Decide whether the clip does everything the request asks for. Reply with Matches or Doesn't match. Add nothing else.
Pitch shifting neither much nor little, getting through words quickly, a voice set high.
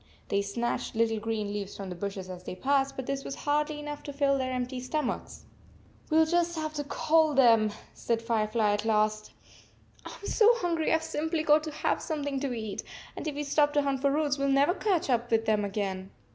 Doesn't match